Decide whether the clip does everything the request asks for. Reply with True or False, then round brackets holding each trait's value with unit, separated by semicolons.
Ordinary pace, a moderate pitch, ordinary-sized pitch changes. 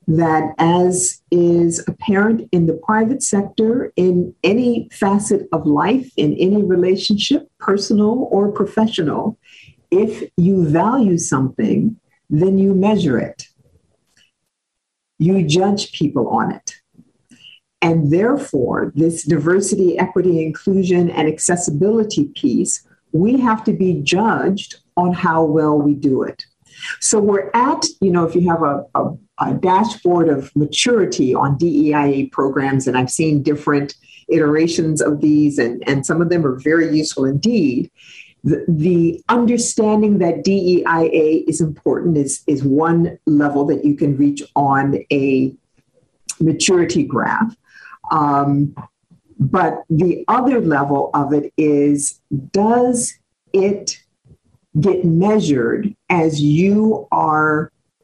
False (125 wpm; 170 Hz; 4.9 semitones)